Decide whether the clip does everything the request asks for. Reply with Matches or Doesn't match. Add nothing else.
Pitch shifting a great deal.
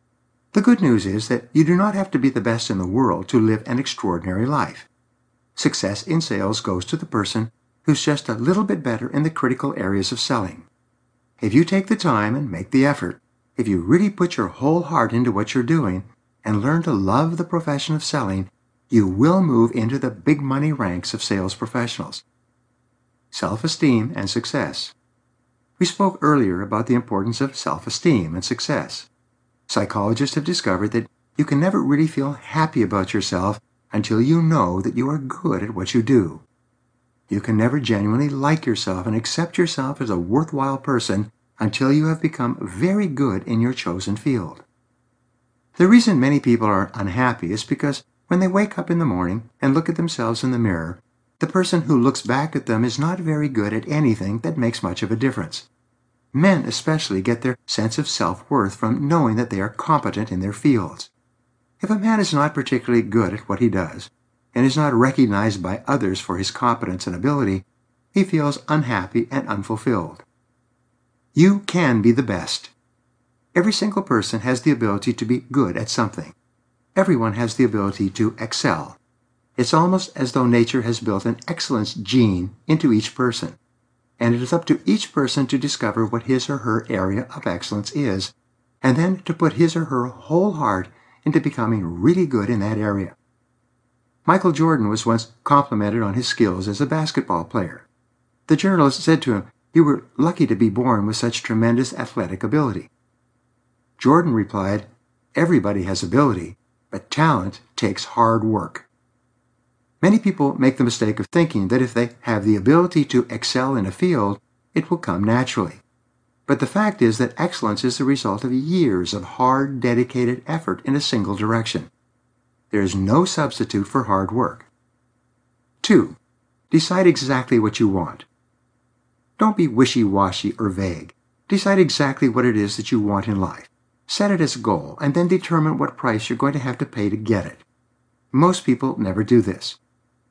Doesn't match